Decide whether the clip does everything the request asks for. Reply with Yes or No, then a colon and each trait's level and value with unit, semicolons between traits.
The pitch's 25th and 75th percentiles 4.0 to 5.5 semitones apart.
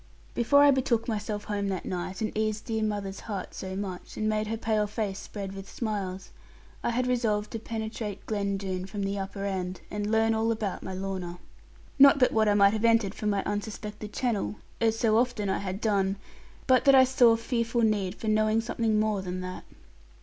No: narrow, 2.4 semitones